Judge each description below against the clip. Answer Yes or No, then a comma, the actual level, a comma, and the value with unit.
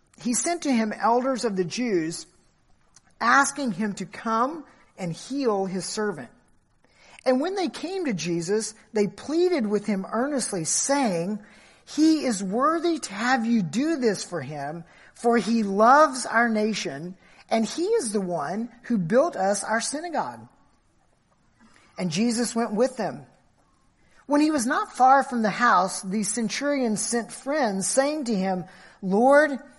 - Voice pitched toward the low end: No, high, 230 Hz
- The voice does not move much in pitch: No, wide, 5.5 semitones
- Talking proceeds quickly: No, average, 150 wpm